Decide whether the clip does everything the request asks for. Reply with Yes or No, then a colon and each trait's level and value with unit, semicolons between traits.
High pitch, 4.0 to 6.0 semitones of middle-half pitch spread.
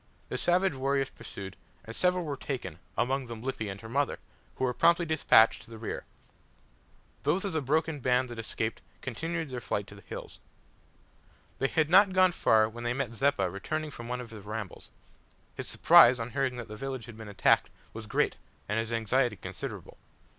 No: low, 125 Hz; average, 4.4 semitones